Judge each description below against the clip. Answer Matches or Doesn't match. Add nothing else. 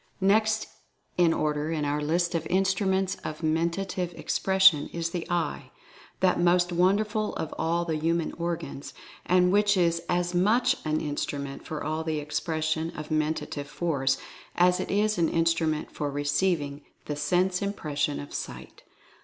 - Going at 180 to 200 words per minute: Doesn't match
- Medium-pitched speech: Matches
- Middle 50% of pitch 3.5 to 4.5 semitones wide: Doesn't match